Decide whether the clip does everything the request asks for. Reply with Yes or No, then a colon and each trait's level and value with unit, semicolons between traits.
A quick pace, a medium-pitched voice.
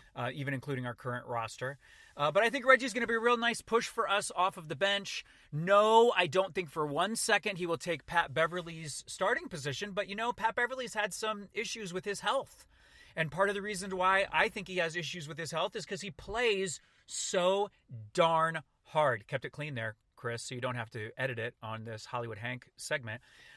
Yes: fast, 220 wpm; medium, 175 Hz